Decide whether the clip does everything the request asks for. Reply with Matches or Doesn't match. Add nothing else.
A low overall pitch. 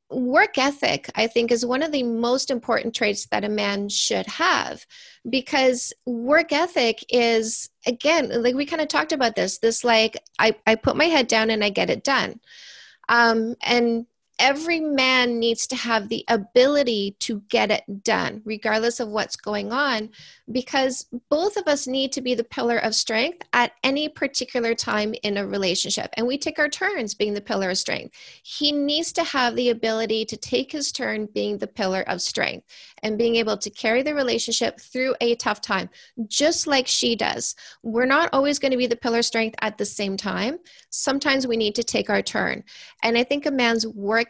Doesn't match